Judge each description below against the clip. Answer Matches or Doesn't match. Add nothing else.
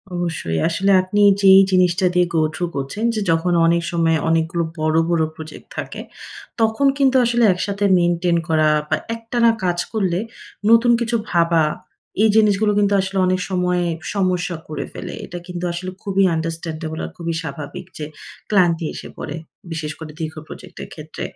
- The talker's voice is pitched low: Doesn't match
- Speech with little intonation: Doesn't match